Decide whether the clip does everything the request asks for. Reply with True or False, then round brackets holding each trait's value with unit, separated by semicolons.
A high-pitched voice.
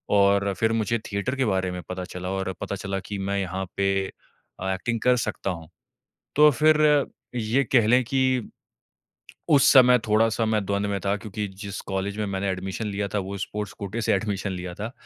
False (100 Hz)